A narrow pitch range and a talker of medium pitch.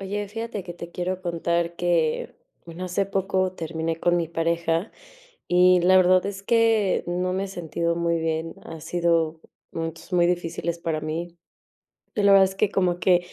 Yes: narrow, 2.0 semitones; medium, 175 Hz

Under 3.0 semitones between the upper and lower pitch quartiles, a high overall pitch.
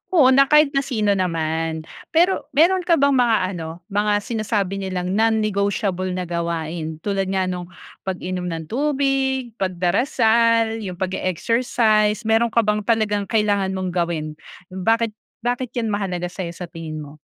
No: average, 4.4 semitones; high, 205 Hz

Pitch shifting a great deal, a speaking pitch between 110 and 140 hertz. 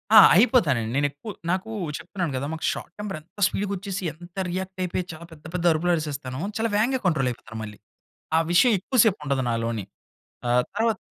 No: wide, 6.1 semitones; medium, 175 Hz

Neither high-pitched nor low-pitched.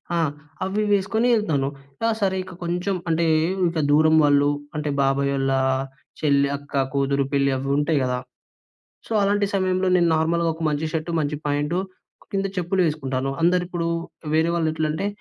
Yes: medium, 160 Hz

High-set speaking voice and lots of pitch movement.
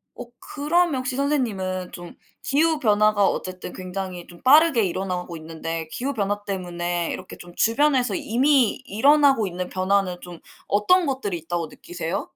Yes: high, 200 Hz; wide, 7.0 semitones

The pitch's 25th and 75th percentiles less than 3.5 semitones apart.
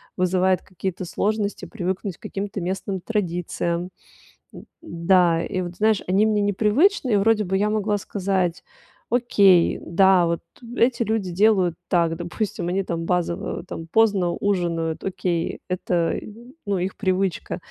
Yes: average, 2.9 semitones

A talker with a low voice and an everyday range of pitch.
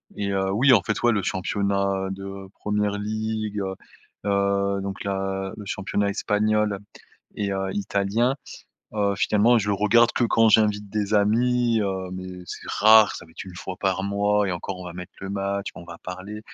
No: low, 100 Hz; narrow, 1.6 semitones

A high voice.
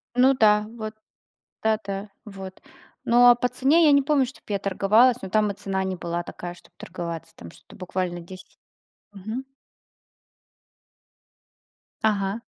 Yes: high, 205 Hz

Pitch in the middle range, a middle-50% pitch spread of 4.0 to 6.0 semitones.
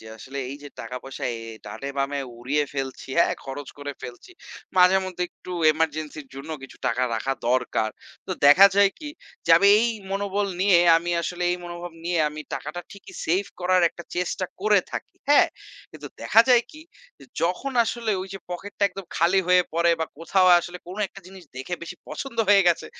Yes: medium, 175 Hz; average, 5.2 semitones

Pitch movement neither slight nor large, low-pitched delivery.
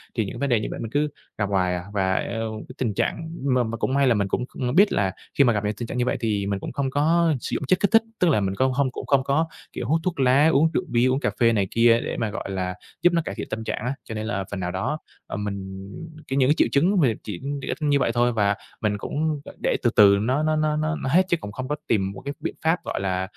No: wide, 5.9 semitones; low, 125 Hz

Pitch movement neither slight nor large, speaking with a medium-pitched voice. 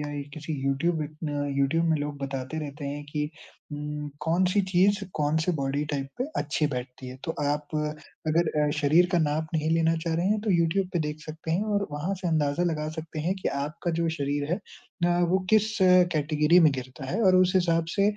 Yes: average, 3.0 semitones; medium, 155 Hz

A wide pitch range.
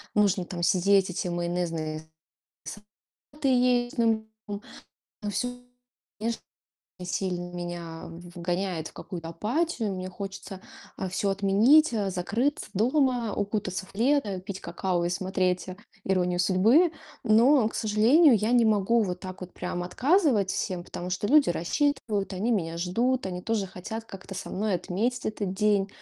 No: average, 4.2 semitones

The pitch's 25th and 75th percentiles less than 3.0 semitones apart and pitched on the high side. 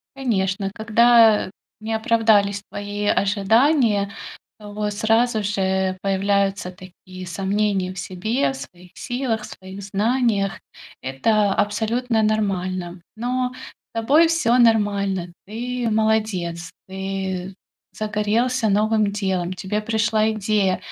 Yes: narrow, 2.6 semitones; high, 210 Hz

